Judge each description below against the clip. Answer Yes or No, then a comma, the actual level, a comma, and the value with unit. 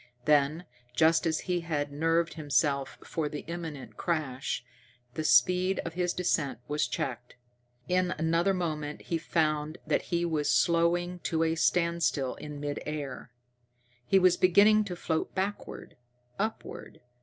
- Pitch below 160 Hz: No, medium, 165 Hz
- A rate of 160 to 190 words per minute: No, average, 140 wpm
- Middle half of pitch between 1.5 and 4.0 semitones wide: Yes, average, 2.9 semitones